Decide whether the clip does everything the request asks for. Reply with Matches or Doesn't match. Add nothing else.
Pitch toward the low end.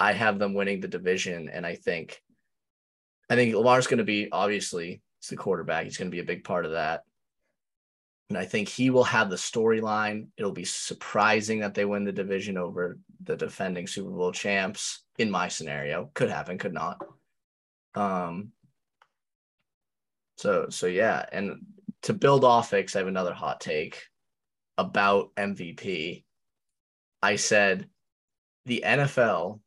Matches